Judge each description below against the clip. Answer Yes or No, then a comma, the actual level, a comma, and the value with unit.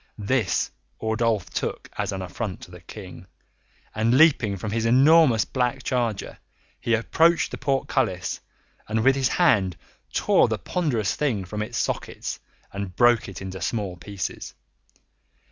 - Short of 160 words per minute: Yes, average, 145 wpm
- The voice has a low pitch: Yes, low, 110 Hz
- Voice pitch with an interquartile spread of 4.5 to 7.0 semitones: Yes, average, 4.9 semitones